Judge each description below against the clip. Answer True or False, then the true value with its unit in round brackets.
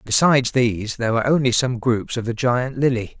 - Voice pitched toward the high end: False (120 Hz)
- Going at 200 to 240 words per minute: True (205 wpm)